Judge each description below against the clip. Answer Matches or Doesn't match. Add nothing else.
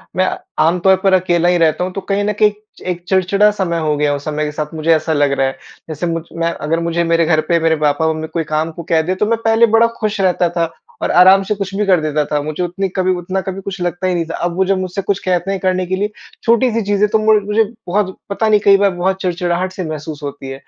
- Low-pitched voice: Doesn't match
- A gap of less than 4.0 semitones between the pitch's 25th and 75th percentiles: Matches